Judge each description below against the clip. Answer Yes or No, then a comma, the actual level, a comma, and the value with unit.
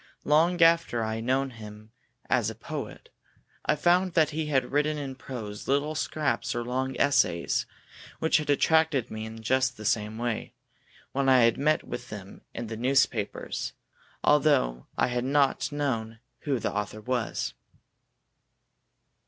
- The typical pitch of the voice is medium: No, low, 130 Hz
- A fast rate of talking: No, average, 155 wpm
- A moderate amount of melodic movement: Yes, average, 4.6 semitones